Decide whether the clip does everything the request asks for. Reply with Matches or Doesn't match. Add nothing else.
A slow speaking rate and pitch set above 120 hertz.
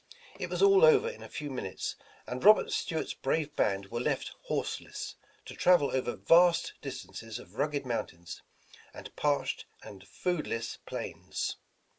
Doesn't match